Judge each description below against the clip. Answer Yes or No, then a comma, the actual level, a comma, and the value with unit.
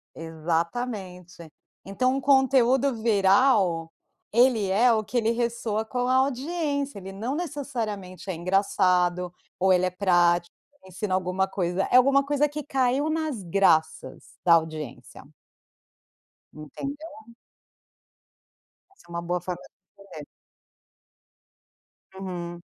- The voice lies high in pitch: Yes, high, 200 Hz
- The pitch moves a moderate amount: No, wide, 6.3 semitones